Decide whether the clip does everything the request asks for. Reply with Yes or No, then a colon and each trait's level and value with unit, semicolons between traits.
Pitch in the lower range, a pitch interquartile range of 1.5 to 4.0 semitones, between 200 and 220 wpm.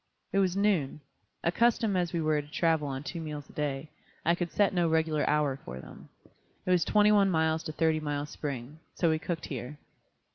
No: medium, 160 Hz; average, 3.0 semitones; fast, 205 wpm